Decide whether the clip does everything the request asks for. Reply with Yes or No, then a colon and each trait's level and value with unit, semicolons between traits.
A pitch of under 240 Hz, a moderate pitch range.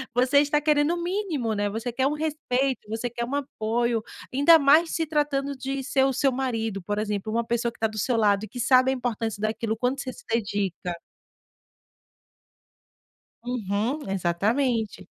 No: high, 245 Hz; average, 4.2 semitones